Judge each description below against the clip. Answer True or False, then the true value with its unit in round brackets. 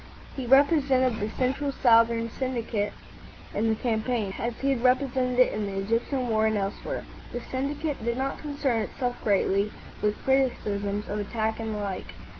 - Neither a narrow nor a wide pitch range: True (3.6 semitones)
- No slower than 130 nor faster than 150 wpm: False (165 wpm)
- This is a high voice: True (235 Hz)